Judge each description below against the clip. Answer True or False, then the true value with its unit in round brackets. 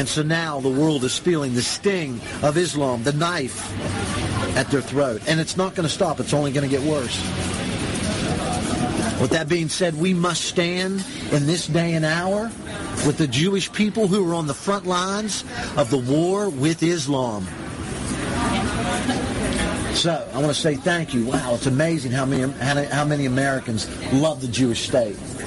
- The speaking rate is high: False (175 wpm)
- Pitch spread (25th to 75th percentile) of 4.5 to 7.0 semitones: True (5.1 semitones)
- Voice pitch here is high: False (145 Hz)